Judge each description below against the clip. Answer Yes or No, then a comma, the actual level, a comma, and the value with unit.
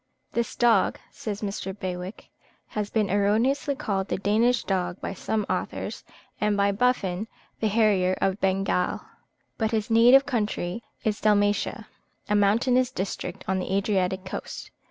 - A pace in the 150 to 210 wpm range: No, average, 140 wpm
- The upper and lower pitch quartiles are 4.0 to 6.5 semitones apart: No, average, 2.7 semitones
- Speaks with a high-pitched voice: Yes, high, 205 Hz